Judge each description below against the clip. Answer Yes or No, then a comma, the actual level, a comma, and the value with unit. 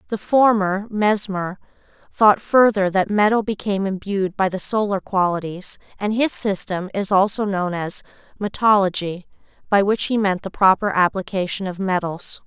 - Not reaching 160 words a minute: Yes, average, 145 wpm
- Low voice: No, high, 195 Hz